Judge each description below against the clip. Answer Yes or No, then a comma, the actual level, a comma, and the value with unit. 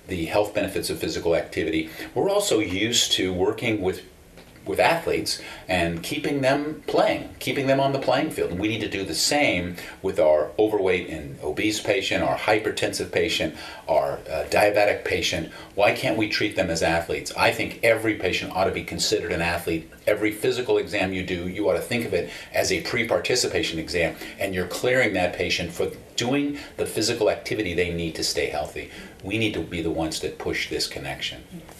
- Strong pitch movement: Yes, wide, 8.3 semitones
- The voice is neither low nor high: No, low, 105 Hz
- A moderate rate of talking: Yes, average, 190 wpm